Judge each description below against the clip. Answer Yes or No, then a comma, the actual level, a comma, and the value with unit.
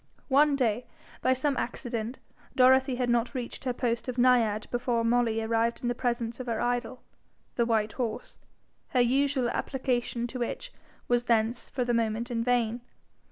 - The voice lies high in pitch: Yes, high, 240 Hz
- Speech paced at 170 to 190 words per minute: No, average, 160 wpm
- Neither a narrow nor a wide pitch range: No, narrow, 1.7 semitones